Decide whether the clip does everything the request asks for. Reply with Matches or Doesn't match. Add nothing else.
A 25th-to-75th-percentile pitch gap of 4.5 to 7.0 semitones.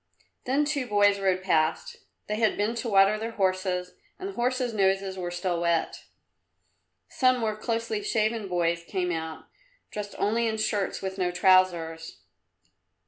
Doesn't match